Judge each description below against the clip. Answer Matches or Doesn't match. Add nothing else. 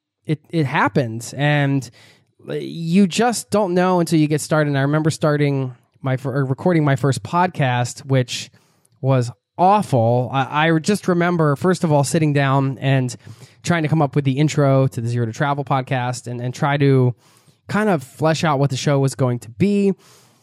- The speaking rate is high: Doesn't match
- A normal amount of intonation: Matches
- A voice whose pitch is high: Doesn't match